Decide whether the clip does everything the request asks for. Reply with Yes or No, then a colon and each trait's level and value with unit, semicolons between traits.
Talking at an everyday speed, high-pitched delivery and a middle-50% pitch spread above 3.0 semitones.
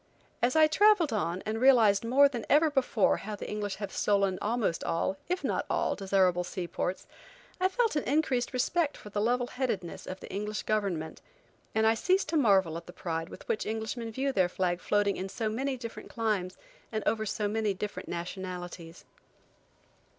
Yes: average, 185 wpm; high, 215 Hz; average, 5.0 semitones